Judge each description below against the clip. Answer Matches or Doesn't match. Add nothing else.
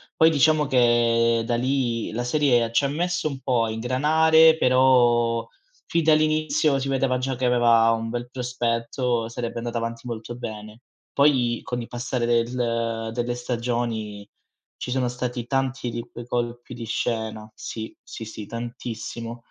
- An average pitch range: Doesn't match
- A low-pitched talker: Matches